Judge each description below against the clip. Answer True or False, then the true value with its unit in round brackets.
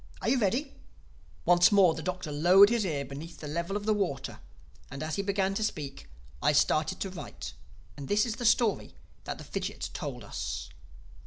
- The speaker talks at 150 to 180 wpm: False (190 wpm)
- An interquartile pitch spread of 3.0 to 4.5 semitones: False (5.0 semitones)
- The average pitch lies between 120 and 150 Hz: False (185 Hz)